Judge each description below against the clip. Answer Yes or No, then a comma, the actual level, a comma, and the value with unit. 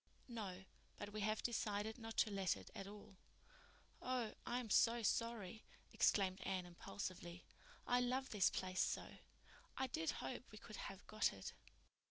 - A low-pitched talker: No, high, 210 Hz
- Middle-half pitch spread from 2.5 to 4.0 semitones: Yes, average, 3.5 semitones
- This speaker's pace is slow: No, average, 155 wpm